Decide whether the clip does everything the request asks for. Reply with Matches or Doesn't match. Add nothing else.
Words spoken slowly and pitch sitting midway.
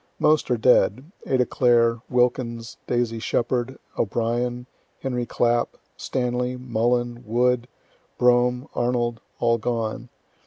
Doesn't match